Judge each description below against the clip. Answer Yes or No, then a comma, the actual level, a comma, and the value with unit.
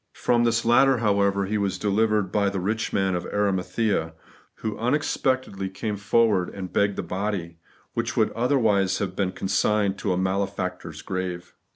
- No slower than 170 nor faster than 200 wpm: No, average, 160 wpm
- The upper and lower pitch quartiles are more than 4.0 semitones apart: No, average, 2.7 semitones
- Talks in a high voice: No, low, 100 Hz